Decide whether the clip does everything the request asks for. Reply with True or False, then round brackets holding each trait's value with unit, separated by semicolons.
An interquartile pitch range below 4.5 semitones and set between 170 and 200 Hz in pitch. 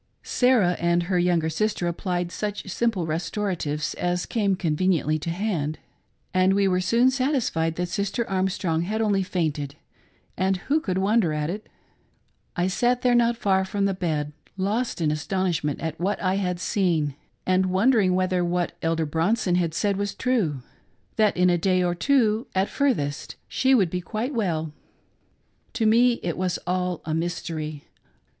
True (3.8 semitones; 185 Hz)